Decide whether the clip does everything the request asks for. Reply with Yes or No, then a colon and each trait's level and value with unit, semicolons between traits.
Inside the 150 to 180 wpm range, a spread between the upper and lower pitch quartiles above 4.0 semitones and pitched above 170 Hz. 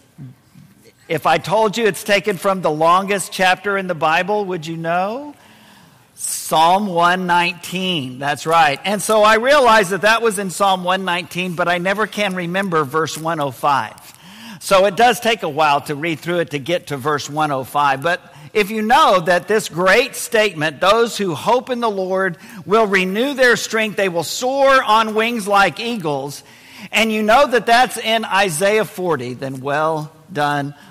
Yes: average, 170 wpm; average, 5.2 semitones; high, 190 Hz